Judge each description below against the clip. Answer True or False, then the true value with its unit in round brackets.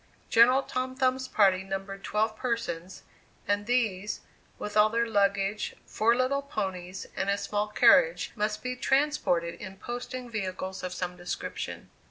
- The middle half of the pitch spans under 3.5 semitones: False (4.4 semitones)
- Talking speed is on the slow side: False (145 wpm)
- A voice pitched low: False (210 Hz)